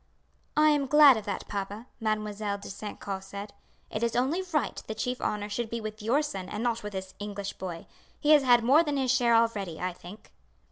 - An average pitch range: Yes, average, 3.8 semitones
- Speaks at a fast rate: Yes, fast, 220 wpm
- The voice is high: Yes, high, 215 Hz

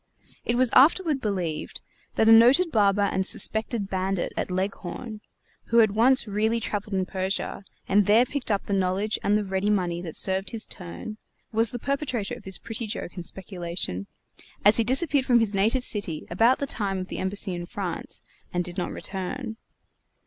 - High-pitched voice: Yes, high, 205 Hz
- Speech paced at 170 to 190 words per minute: Yes, average, 185 wpm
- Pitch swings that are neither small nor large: Yes, average, 3.5 semitones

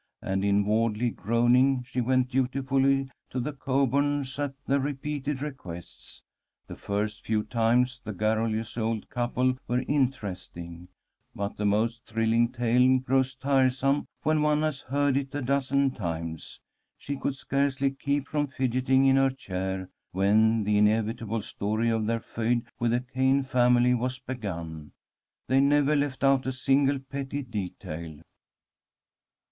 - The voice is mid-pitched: No, low, 125 Hz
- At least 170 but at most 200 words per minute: No, average, 140 wpm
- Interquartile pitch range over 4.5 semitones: No, average, 3.7 semitones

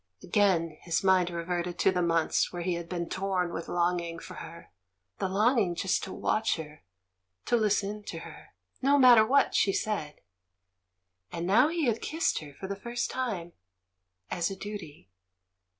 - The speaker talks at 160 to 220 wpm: Yes, average, 175 wpm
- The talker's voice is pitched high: No, medium, 180 Hz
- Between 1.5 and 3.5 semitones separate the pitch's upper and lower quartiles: No, average, 3.9 semitones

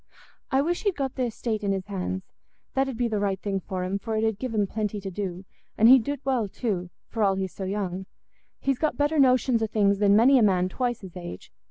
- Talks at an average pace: No, fast, 245 wpm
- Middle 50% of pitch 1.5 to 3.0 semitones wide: No, average, 4.6 semitones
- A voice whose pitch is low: No, high, 210 Hz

